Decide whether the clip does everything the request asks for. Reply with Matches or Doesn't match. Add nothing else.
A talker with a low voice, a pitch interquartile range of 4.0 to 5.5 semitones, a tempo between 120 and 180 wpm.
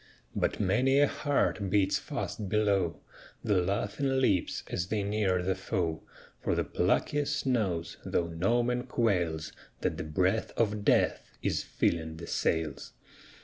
Matches